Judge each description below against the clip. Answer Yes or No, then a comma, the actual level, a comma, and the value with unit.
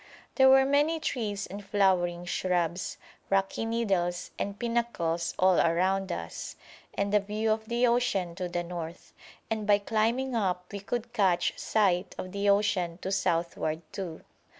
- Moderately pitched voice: No, high, 195 Hz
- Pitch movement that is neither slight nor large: Yes, average, 3.8 semitones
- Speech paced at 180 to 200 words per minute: No, average, 150 wpm